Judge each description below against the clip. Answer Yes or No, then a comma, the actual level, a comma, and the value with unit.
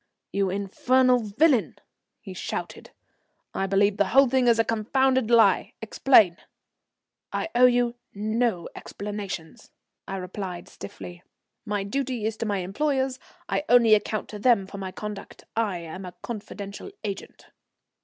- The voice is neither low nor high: No, high, 210 Hz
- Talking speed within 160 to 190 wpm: No, average, 140 wpm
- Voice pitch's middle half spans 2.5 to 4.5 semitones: Yes, average, 3.8 semitones